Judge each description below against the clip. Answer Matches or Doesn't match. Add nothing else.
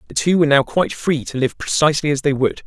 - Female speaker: Doesn't match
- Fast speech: Matches